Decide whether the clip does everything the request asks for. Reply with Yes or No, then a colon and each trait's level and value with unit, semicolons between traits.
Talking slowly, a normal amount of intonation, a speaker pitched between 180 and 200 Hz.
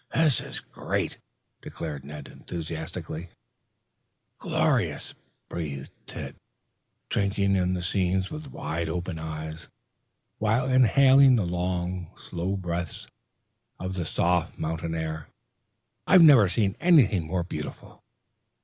No: slow, 105 wpm; average, 4.2 semitones; very low, 90 Hz